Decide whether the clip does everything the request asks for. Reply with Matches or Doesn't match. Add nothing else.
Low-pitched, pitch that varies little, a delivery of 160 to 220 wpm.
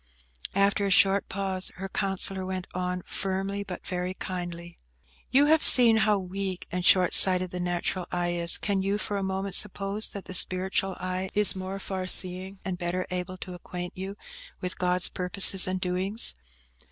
Doesn't match